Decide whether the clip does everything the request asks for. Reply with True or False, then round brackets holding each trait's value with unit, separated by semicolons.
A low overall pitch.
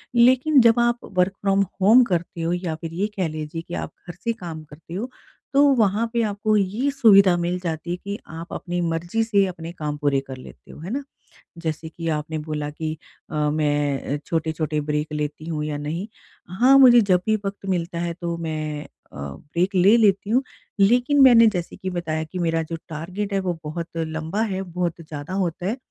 False (175 Hz)